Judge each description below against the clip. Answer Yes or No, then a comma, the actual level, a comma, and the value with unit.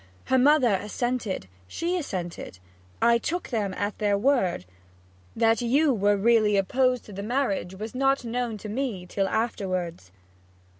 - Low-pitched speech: No, high, 225 Hz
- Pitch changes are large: No, average, 4.3 semitones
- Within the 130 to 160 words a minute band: Yes, average, 145 wpm